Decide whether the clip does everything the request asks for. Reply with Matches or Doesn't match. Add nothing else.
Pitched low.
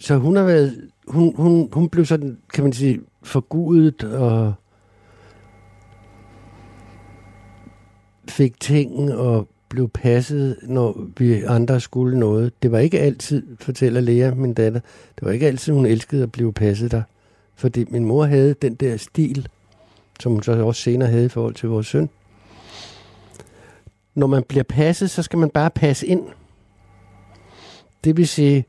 Matches